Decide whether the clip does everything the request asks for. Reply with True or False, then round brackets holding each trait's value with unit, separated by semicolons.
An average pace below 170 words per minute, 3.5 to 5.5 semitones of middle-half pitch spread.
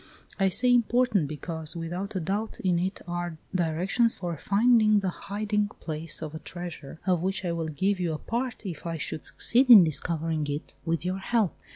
False (190 wpm; 4.2 semitones)